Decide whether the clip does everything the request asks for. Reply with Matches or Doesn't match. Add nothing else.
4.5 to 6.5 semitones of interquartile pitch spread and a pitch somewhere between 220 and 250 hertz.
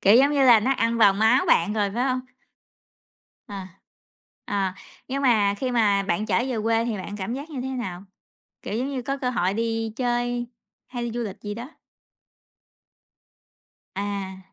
Doesn't match